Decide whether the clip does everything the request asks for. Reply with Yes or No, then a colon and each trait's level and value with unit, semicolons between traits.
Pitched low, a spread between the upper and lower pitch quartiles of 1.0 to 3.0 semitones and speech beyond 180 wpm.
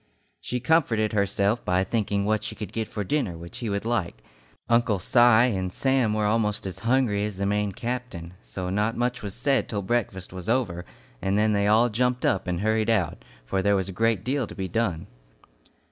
No: low, 105 Hz; average, 3.6 semitones; average, 200 wpm